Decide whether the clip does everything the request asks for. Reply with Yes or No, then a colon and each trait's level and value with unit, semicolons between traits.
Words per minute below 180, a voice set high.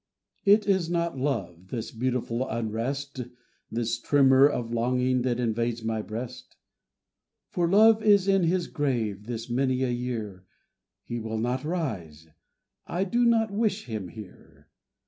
No: average, 140 wpm; low, 125 Hz